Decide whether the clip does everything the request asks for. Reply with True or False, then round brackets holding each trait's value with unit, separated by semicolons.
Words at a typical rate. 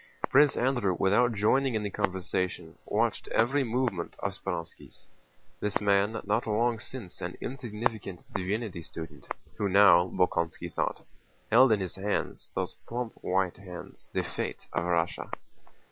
False (130 wpm)